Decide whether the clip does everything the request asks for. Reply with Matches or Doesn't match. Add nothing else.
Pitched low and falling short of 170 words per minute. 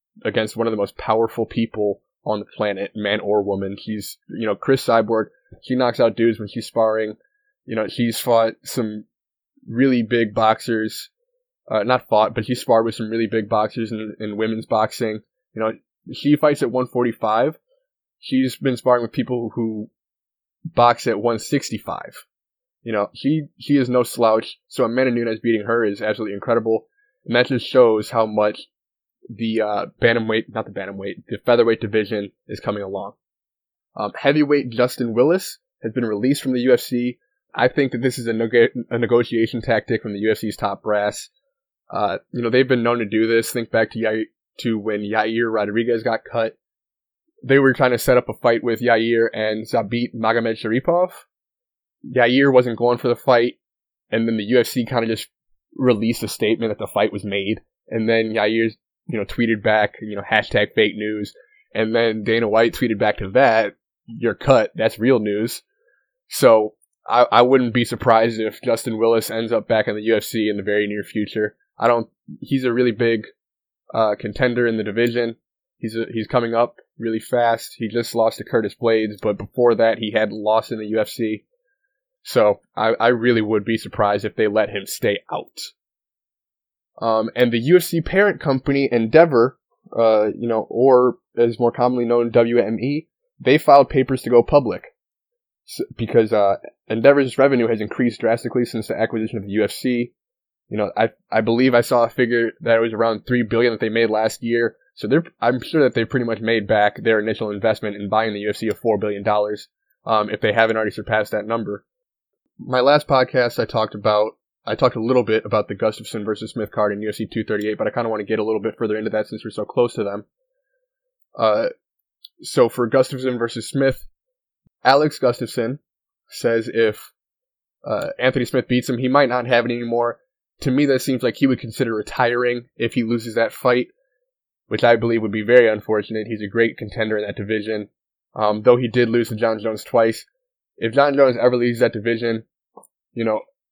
Doesn't match